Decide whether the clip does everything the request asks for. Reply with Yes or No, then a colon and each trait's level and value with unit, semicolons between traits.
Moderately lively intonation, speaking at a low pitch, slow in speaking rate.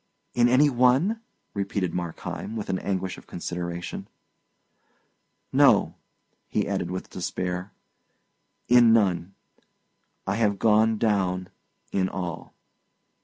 Yes: average, 4.0 semitones; low, 100 Hz; slow, 105 wpm